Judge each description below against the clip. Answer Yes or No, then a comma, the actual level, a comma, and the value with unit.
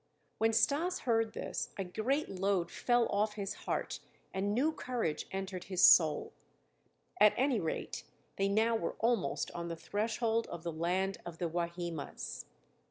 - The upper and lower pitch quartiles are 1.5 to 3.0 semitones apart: No, average, 4.7 semitones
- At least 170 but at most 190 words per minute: No, average, 155 wpm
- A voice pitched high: Yes, high, 200 Hz